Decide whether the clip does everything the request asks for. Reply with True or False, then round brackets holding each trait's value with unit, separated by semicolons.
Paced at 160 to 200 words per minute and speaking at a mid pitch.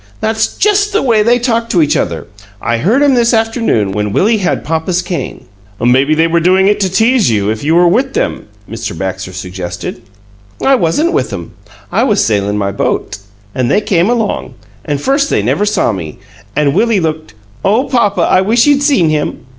True (195 wpm; 180 Hz)